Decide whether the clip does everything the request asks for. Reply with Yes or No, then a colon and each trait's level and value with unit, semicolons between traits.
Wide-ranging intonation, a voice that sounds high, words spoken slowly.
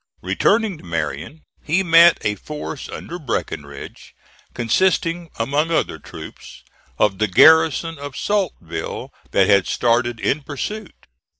No: wide, 8.1 semitones; medium, 145 Hz; slow, 120 wpm